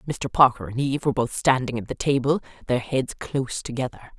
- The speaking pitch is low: Yes, low, 130 Hz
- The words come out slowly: No, average, 200 wpm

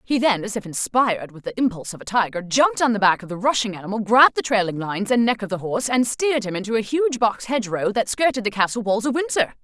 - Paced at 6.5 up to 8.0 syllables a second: Yes, 6.6 syllables/s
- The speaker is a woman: Yes, female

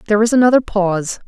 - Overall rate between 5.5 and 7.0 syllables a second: No, 7.7 syllables/s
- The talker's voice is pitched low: No, high, 215 Hz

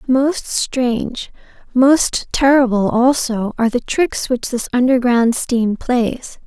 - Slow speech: Yes, slow, 120 wpm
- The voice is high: Yes, high, 245 Hz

